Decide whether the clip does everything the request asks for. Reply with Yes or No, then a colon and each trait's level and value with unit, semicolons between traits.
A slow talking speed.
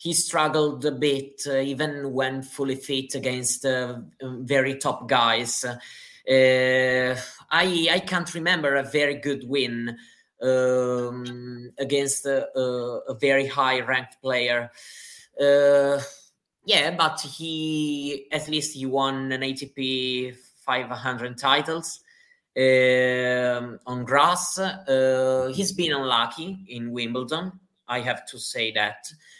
Yes: slow, 120 wpm